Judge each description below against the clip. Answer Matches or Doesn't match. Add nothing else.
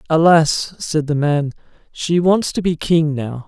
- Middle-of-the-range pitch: Matches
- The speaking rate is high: Doesn't match